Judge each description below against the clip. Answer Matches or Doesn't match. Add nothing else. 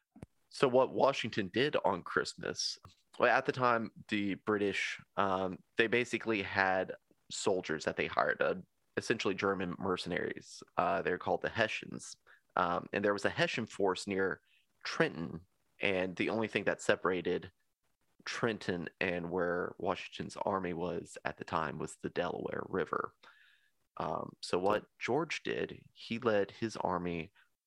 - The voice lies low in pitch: Matches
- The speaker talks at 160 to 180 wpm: Doesn't match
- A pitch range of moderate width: Matches